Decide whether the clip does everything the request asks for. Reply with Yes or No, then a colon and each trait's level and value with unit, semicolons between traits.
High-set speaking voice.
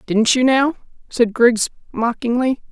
Yes: high, 240 Hz